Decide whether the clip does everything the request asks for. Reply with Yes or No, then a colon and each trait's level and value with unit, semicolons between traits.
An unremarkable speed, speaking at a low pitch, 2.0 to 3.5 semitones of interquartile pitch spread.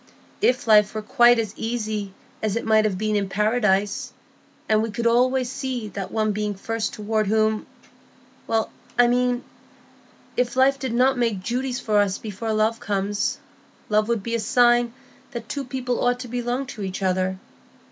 No: average, 170 wpm; high, 225 Hz; average, 2.7 semitones